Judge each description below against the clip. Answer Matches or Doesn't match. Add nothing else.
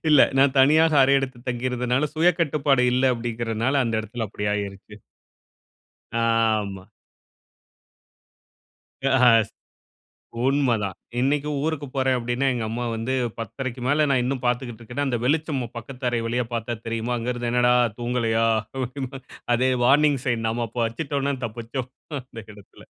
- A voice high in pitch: Doesn't match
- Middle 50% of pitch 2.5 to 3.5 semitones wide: Matches